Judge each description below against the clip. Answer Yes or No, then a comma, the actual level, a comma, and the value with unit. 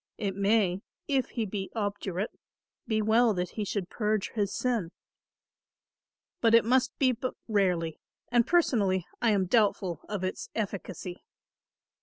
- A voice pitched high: Yes, high, 210 Hz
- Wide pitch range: No, average, 3.5 semitones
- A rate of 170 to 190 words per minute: No, average, 140 wpm